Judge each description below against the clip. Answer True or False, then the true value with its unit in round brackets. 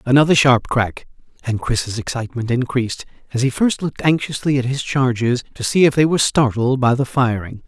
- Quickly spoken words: False (190 wpm)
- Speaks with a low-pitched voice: True (130 Hz)